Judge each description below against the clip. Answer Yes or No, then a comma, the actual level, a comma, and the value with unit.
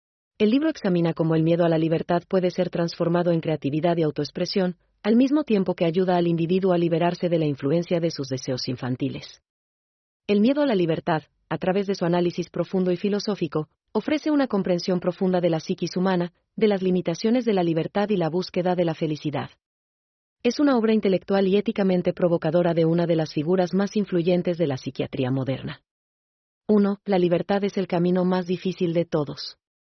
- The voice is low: No, medium, 175 Hz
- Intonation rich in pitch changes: No, average, 2.7 semitones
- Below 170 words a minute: No, average, 185 wpm